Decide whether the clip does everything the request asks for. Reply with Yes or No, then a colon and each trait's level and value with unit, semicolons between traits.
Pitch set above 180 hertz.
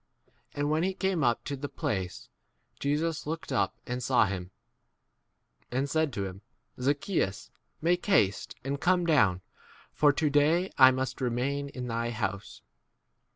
No: medium, 140 Hz